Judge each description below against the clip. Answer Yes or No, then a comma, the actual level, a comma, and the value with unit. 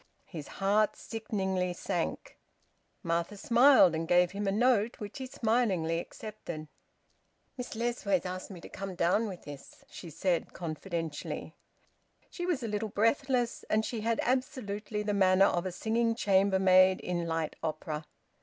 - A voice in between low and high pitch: No, high, 195 Hz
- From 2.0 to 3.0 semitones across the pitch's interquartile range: No, average, 4.3 semitones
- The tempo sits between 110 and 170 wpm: Yes, average, 145 wpm